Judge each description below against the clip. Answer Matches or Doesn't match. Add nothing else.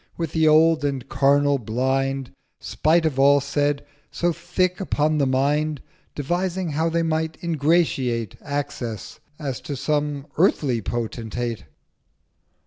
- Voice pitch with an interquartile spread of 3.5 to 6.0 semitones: Doesn't match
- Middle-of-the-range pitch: Matches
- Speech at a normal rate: Doesn't match